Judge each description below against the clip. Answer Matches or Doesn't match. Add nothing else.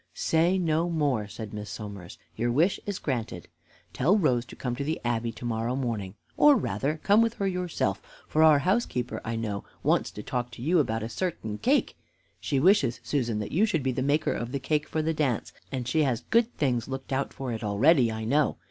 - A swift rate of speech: Matches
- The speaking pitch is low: Matches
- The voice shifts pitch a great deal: Matches